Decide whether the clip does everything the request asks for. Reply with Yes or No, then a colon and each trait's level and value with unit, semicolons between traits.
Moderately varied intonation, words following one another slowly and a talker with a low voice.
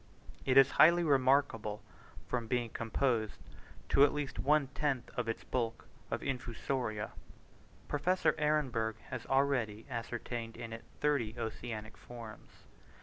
Yes: average, 3.6 semitones; slow, 125 wpm; low, 120 Hz